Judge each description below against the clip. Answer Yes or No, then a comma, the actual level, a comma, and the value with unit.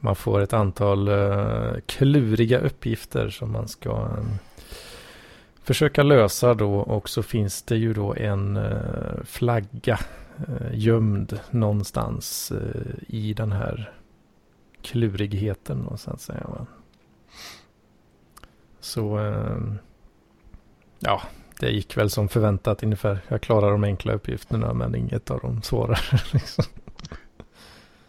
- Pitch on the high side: No, low, 105 Hz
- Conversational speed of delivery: No, slow, 110 wpm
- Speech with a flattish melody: Yes, narrow, 2.2 semitones